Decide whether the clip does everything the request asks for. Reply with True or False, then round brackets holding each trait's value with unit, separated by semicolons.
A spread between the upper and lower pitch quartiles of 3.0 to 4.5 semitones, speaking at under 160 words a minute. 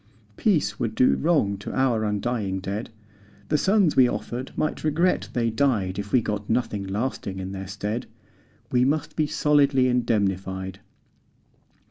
False (5.1 semitones; 145 wpm)